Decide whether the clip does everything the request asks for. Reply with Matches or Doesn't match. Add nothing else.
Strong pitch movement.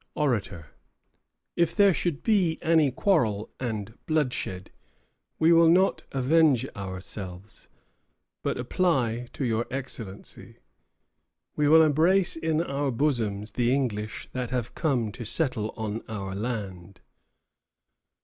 Matches